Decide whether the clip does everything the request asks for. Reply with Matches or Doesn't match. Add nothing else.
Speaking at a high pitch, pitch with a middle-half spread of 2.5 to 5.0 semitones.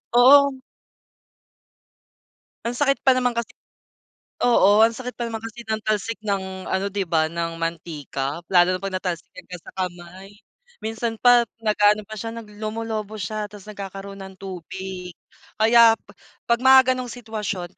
Matches